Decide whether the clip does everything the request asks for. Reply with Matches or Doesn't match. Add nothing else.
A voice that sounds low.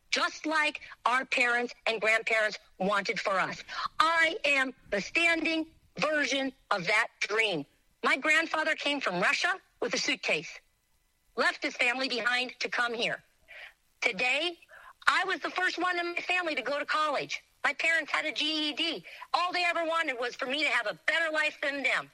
Doesn't match